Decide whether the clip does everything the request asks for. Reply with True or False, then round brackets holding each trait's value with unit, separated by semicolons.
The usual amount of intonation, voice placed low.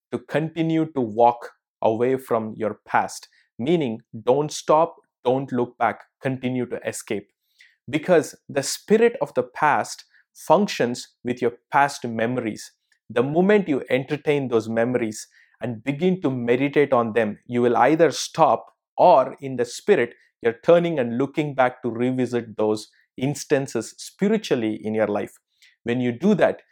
True (3.5 semitones; 125 Hz)